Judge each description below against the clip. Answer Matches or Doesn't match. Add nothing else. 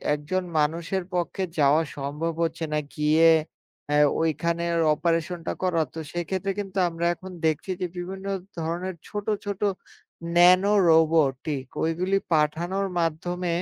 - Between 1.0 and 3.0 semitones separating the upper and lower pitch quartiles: Matches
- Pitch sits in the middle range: Matches